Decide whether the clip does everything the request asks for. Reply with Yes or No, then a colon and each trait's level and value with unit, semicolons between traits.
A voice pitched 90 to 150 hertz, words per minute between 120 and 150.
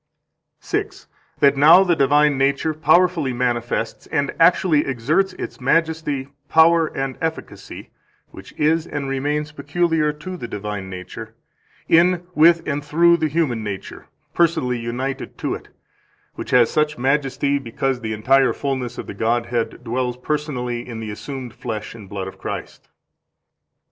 Yes: low, 135 Hz; average, 145 wpm